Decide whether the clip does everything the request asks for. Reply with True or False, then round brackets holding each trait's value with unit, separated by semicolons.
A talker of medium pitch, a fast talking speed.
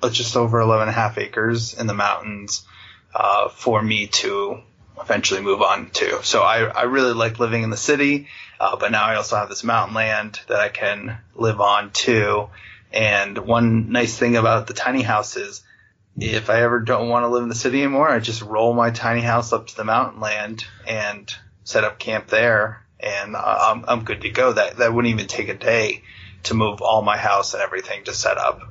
False (110 Hz; 215 wpm)